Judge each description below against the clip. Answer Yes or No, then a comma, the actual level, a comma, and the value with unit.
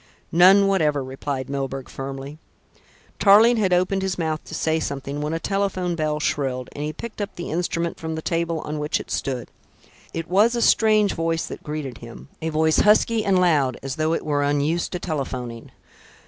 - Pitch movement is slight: No, average, 4.3 semitones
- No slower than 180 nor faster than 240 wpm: Yes, average, 190 wpm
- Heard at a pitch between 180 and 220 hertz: No, medium, 160 Hz